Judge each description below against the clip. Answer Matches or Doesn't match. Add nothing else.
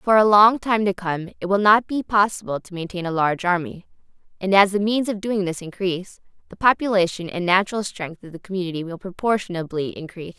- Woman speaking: Matches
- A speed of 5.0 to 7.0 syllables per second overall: Matches